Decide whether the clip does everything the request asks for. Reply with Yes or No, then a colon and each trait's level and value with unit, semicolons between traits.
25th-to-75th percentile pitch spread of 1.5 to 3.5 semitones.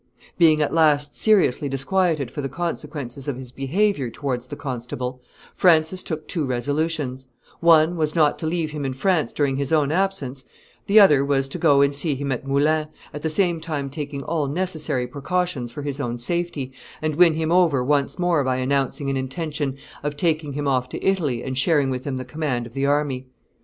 Yes: average, 3.2 semitones